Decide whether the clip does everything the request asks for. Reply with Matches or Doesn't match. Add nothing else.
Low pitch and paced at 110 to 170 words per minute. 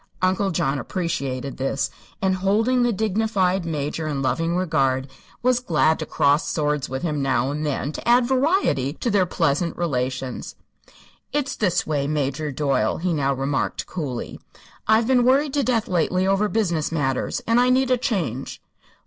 Doesn't match